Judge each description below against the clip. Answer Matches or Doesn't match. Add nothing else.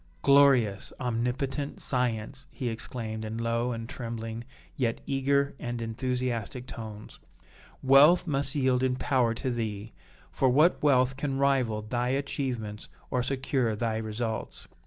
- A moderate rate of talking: Doesn't match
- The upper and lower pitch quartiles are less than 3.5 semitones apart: Matches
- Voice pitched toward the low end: Matches